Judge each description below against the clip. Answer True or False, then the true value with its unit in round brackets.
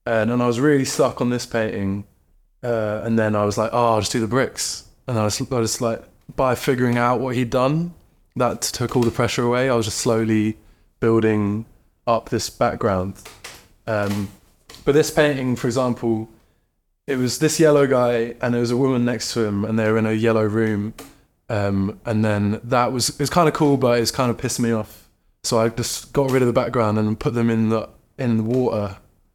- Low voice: True (115 Hz)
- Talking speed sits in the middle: False (215 wpm)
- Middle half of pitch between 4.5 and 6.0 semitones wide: False (2.7 semitones)